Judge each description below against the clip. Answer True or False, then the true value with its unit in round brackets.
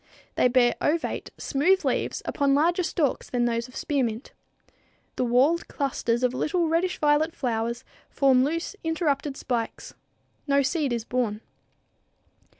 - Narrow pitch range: False (4.6 semitones)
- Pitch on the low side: False (275 Hz)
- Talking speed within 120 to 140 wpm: True (135 wpm)